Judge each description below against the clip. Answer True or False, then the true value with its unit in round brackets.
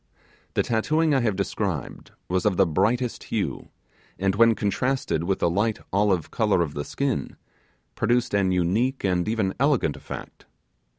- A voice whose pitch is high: False (105 Hz)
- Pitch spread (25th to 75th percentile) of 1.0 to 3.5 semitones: False (4.4 semitones)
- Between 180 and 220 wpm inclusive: False (155 wpm)